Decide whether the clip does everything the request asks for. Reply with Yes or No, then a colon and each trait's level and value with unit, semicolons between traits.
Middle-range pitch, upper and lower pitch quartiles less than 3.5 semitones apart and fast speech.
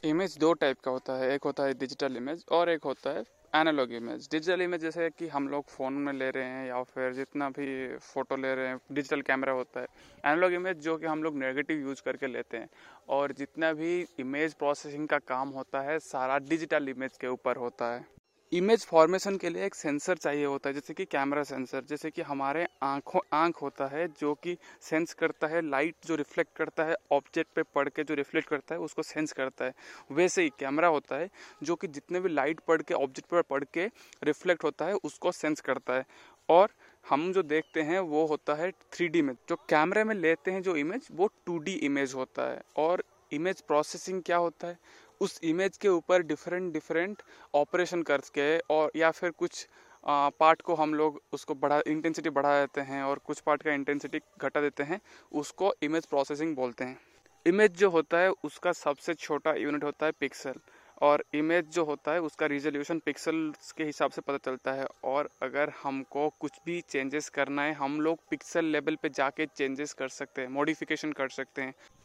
Yes: medium, 150 Hz; average, 3.1 semitones; fast, 200 wpm